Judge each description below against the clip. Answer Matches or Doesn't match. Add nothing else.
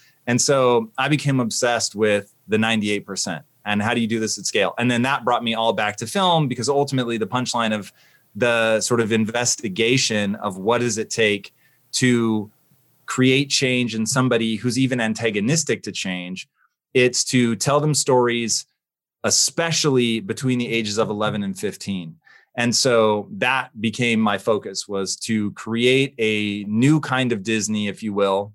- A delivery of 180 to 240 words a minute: Doesn't match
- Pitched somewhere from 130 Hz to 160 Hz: Doesn't match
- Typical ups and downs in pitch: Matches